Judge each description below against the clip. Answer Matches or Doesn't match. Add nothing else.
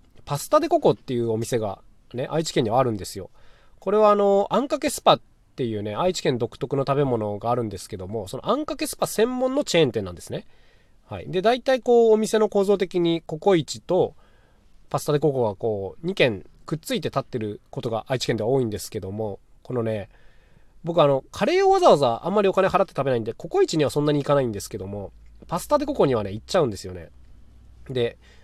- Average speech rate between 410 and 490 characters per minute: Matches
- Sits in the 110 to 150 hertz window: Matches